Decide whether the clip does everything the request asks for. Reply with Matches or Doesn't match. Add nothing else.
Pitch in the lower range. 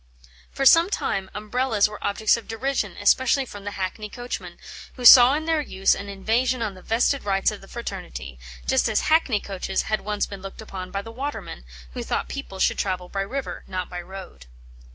Doesn't match